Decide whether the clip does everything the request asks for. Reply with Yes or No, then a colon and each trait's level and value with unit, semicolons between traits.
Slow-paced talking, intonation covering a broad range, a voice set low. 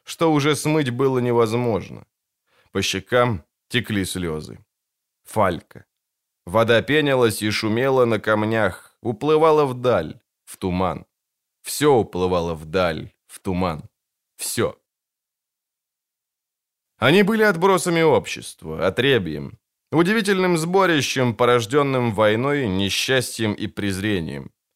Yes: slow, 90 wpm; wide, 6.4 semitones; low, 120 Hz